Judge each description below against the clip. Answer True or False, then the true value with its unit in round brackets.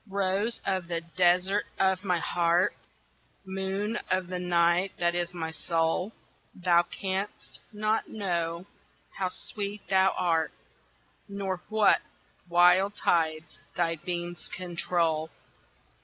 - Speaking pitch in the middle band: True (180 Hz)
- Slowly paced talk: True (110 wpm)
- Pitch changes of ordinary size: False (2.0 semitones)